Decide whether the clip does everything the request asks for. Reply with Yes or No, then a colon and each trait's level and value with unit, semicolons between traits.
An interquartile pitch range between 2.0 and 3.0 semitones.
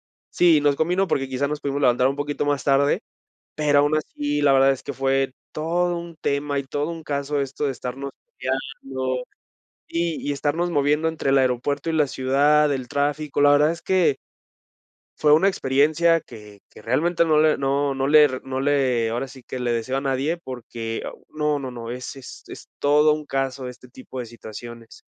Yes: narrow, 2.4 semitones